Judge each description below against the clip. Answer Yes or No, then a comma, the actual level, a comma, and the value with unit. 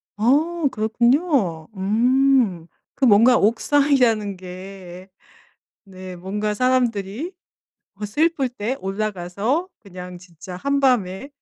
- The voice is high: Yes, high, 215 Hz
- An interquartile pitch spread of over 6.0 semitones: No, wide, 5.6 semitones